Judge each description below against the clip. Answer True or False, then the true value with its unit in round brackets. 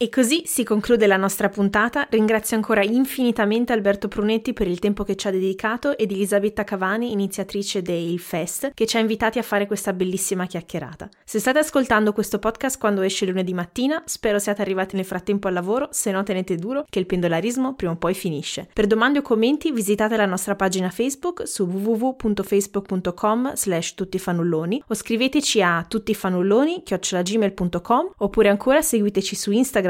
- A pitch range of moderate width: True (3.2 semitones)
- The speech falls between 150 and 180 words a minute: True (165 wpm)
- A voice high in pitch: True (210 Hz)